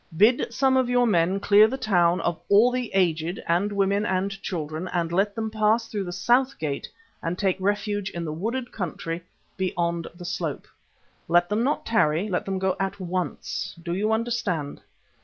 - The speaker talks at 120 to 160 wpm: No, average, 180 wpm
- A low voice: No, high, 195 Hz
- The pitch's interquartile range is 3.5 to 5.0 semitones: Yes, average, 4.1 semitones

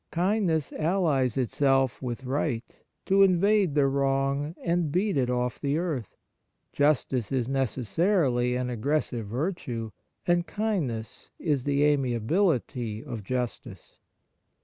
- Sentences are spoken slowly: Yes, slow, 115 wpm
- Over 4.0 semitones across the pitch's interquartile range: Yes, wide, 5.4 semitones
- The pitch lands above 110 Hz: Yes, medium, 140 Hz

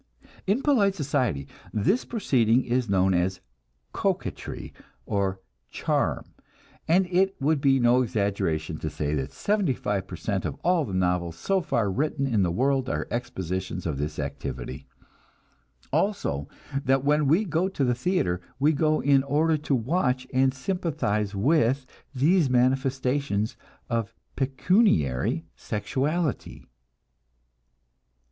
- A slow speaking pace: Yes, slow, 130 wpm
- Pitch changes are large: Yes, wide, 7.9 semitones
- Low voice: Yes, low, 130 Hz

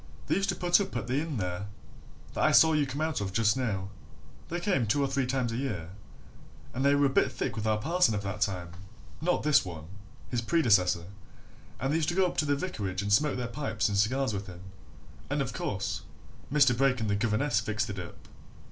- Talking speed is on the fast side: Yes, fast, 230 wpm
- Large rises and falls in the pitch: Yes, wide, 6.1 semitones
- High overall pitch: No, low, 125 Hz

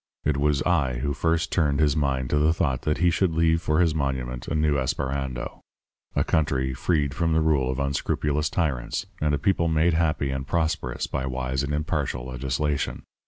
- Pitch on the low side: Yes, very low, 75 Hz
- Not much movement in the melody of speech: No, average, 3.2 semitones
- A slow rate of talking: No, average, 190 wpm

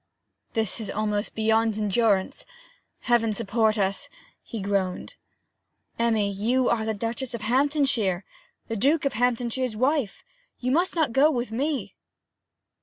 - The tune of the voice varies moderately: Yes, average, 3.3 semitones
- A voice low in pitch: No, high, 230 Hz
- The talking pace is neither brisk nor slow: No, slow, 130 wpm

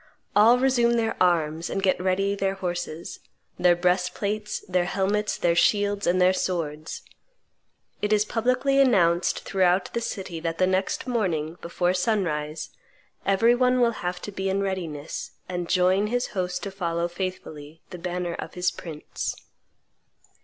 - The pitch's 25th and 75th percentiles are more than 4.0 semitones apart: No, average, 3.0 semitones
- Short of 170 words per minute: Yes, average, 150 wpm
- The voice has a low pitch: No, medium, 185 Hz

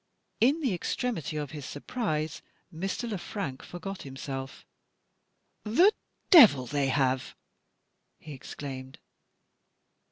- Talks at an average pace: No, slow, 100 wpm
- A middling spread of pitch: No, wide, 7.8 semitones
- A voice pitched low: No, medium, 155 Hz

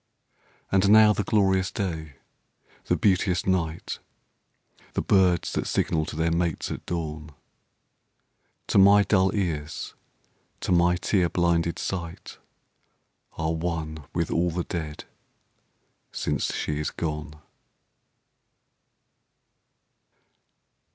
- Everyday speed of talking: No, slow, 105 wpm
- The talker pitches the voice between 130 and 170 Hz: No, very low, 85 Hz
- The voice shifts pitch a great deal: No, average, 2.9 semitones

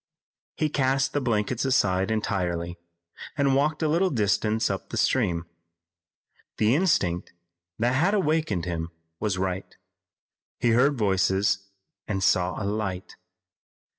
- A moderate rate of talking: No, slow, 125 wpm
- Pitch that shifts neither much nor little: No, wide, 6.4 semitones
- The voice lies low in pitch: Yes, low, 105 Hz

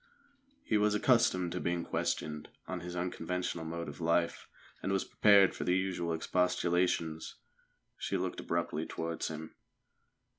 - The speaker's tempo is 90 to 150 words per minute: Yes, average, 140 wpm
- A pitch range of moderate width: No, narrow, 2.0 semitones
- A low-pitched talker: Yes, very low, 85 Hz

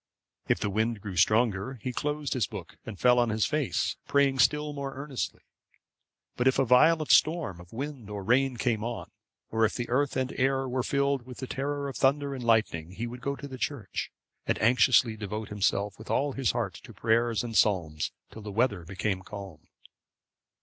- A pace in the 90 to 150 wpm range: No, average, 195 wpm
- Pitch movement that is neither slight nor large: Yes, average, 4.3 semitones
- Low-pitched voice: Yes, low, 120 Hz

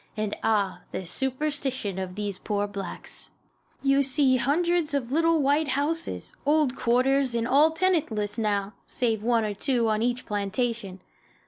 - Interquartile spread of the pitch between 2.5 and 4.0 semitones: No, average, 5.3 semitones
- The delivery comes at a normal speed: Yes, average, 145 wpm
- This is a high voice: Yes, high, 245 Hz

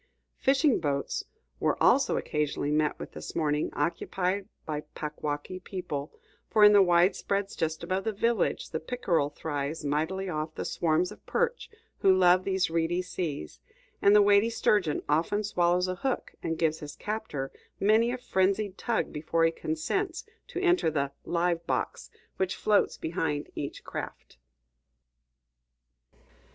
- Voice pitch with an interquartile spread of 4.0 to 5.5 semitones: Yes, average, 4.6 semitones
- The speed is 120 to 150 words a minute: Yes, average, 145 wpm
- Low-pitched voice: No, medium, 180 Hz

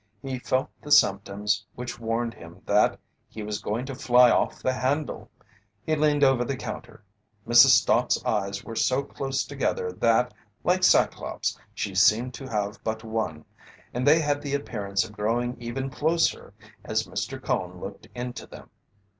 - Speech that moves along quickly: No, average, 165 wpm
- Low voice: Yes, low, 120 Hz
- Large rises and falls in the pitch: No, average, 4.2 semitones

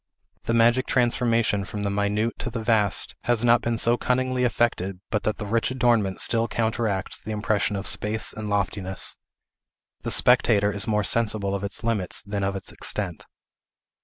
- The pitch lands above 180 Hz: No, low, 110 Hz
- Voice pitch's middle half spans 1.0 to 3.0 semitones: Yes, narrow, 2.6 semitones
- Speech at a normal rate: Yes, average, 170 wpm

